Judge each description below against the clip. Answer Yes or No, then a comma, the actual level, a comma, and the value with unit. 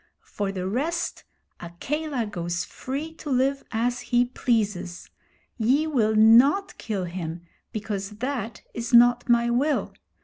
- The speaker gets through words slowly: Yes, slow, 130 wpm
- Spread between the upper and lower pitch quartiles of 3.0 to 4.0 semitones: No, average, 4.4 semitones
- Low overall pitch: No, high, 235 Hz